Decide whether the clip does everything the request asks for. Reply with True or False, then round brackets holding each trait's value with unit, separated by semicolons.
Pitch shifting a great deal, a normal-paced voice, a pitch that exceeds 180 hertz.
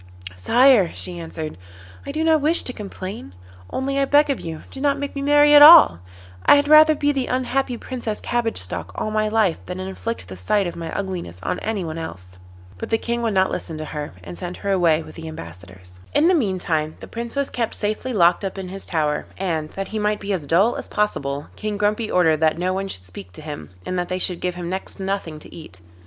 False (6.9 semitones; 235 wpm; 190 Hz)